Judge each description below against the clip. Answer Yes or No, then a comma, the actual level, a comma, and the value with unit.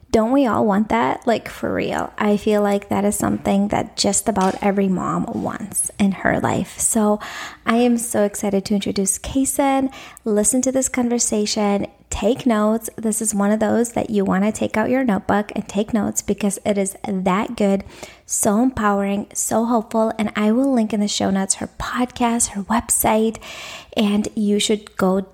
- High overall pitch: Yes, high, 215 Hz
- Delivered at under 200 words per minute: Yes, average, 185 wpm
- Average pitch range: No, narrow, 2.3 semitones